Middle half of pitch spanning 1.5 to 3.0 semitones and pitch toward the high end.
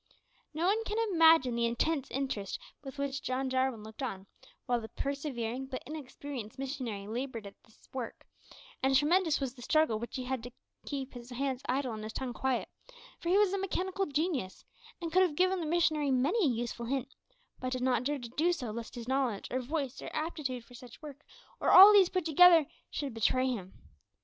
No: average, 4.3 semitones; very high, 265 Hz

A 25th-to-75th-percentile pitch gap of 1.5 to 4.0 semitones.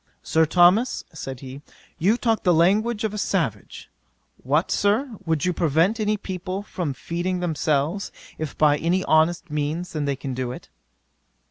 No: average, 4.8 semitones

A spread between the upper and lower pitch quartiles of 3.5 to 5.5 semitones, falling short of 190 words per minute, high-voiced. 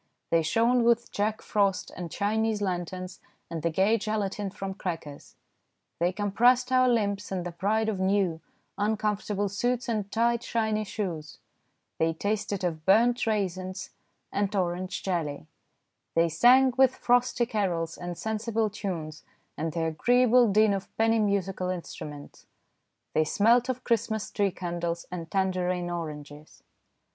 Yes: average, 4.0 semitones; slow, 135 wpm; high, 200 Hz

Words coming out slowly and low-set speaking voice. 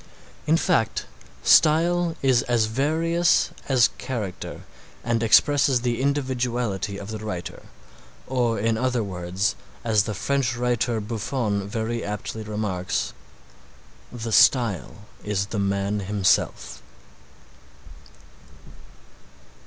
Yes: slow, 100 wpm; low, 115 Hz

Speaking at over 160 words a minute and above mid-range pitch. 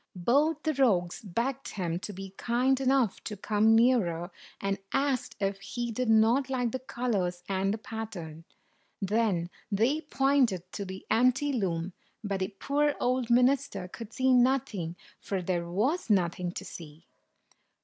No: average, 150 wpm; high, 220 Hz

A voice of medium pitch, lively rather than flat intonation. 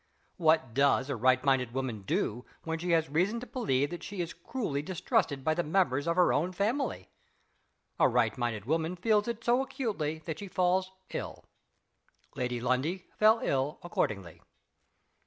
Yes: medium, 160 Hz; wide, 6.3 semitones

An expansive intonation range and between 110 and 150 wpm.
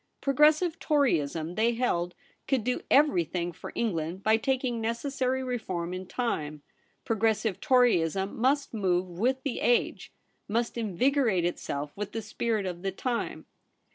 Yes: wide, 6.1 semitones; average, 140 wpm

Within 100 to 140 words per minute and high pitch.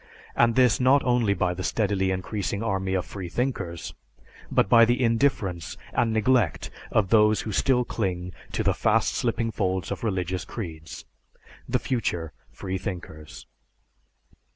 No: slow, 135 wpm; low, 100 Hz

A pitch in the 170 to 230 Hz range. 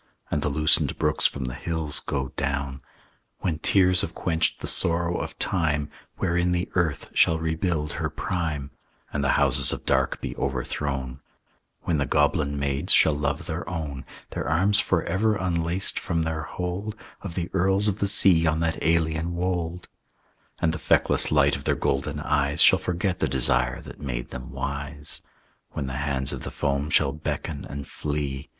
No: very low, 80 Hz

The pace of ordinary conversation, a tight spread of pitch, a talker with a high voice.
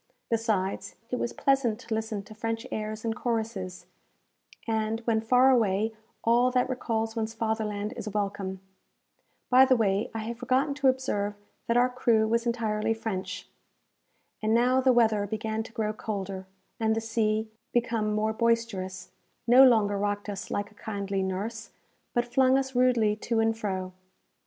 Yes: average, 160 wpm; narrow, 2.2 semitones; high, 220 Hz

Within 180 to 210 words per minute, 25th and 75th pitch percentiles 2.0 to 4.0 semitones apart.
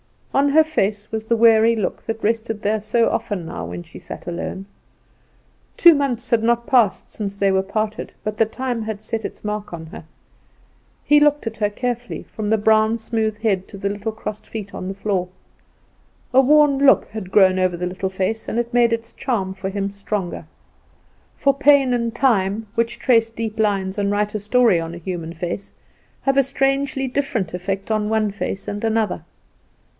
Yes: average, 190 wpm; average, 3.1 semitones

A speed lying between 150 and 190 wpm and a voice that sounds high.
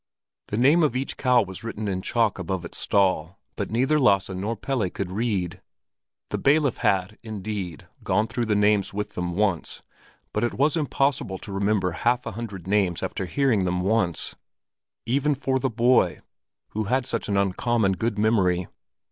No: average, 170 wpm; low, 105 Hz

